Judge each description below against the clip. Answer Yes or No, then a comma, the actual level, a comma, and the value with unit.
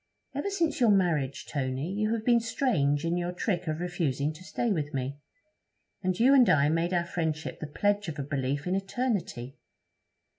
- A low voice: No, medium, 175 Hz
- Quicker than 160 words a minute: Yes, average, 185 wpm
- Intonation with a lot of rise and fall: Yes, wide, 6.1 semitones